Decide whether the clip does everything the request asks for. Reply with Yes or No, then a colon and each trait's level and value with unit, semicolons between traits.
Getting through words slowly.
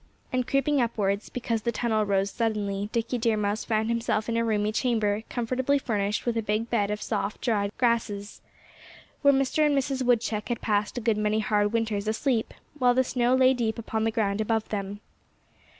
No: average, 190 wpm